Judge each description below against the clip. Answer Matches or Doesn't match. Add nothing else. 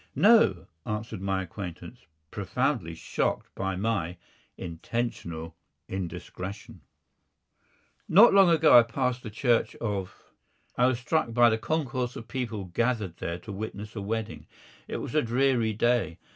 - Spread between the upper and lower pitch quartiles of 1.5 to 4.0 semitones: Doesn't match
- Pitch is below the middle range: Matches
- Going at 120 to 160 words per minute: Matches